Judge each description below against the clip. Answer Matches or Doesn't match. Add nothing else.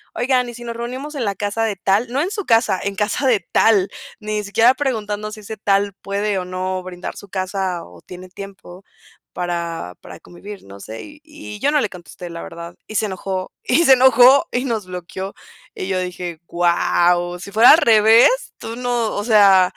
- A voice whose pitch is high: Matches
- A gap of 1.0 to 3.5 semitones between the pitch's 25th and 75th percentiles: Doesn't match